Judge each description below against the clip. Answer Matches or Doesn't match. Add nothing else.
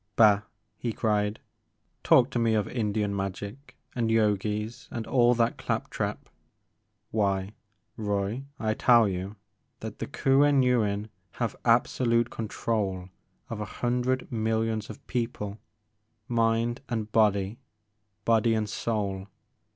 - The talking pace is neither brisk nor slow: Doesn't match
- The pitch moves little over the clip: Matches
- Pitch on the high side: Doesn't match